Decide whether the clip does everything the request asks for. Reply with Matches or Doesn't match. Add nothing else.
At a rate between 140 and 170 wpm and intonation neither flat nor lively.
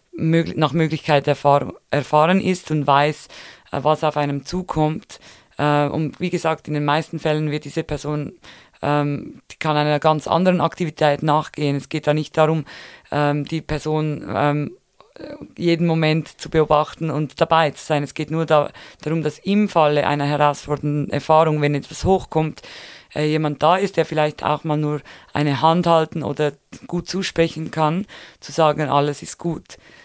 Doesn't match